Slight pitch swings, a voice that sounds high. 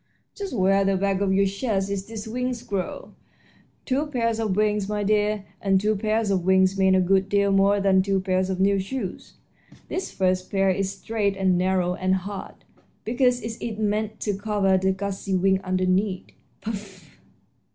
Yes: narrow, 2.0 semitones; high, 195 Hz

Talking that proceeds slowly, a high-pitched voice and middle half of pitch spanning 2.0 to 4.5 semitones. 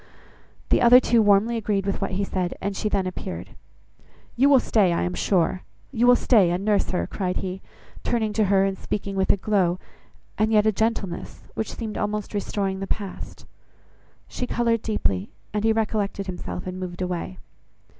No: average, 185 wpm; high, 200 Hz; average, 2.8 semitones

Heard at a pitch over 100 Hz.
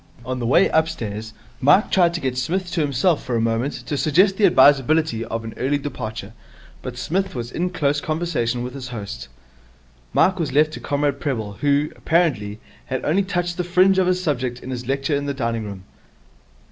Yes: medium, 140 Hz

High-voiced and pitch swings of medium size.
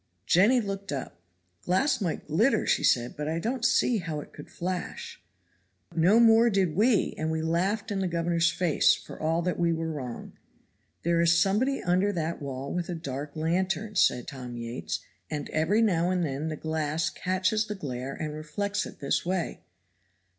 No: medium, 170 Hz; average, 4.3 semitones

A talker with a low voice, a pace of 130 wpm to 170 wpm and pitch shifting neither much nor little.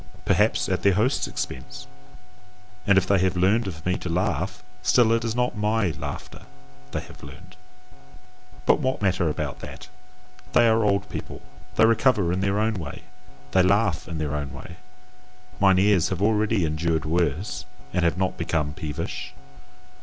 Yes: very low, 95 Hz; average, 165 wpm; average, 4.2 semitones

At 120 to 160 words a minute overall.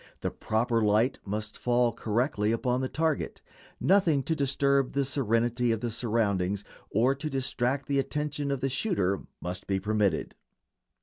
Yes: average, 150 wpm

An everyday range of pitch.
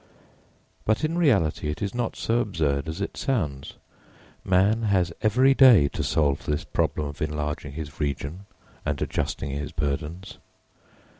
No: wide, 6.5 semitones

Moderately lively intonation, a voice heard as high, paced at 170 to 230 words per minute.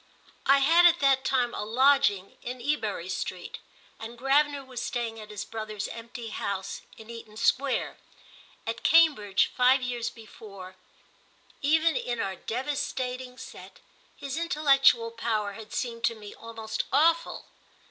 No: average, 3.9 semitones; high, 240 Hz; slow, 135 wpm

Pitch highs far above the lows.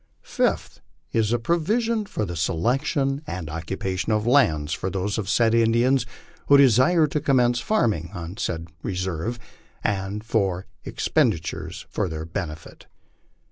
Yes: wide, 6.6 semitones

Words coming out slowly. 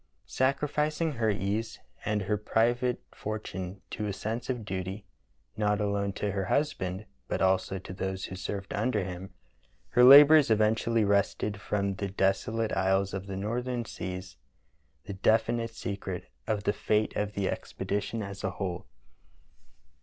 No: average, 155 wpm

